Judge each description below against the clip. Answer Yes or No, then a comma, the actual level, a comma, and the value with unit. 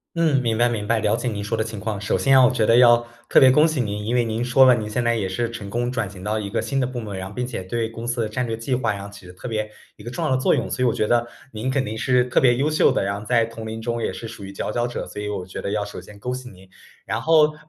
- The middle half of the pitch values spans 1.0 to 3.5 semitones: Yes, average, 3.1 semitones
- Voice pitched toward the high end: No, low, 115 Hz